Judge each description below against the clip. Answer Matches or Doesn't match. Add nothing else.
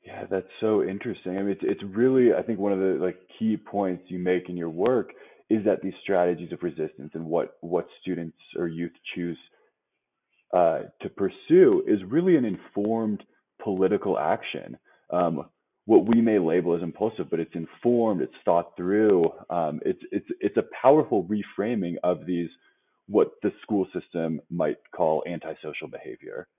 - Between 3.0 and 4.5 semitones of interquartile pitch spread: Matches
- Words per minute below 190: Matches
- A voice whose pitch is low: Matches